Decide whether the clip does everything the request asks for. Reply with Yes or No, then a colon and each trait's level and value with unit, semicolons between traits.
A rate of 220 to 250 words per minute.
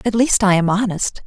Yes: fast, 235 wpm